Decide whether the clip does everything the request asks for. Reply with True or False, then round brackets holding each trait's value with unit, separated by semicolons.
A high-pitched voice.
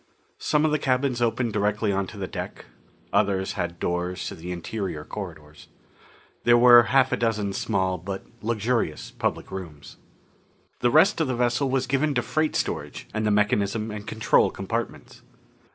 False (110 Hz)